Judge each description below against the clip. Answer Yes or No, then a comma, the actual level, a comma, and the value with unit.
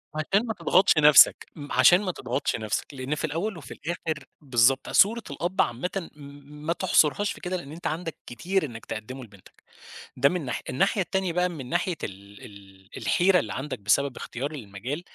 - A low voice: No, medium, 150 Hz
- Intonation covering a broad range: Yes, wide, 6.4 semitones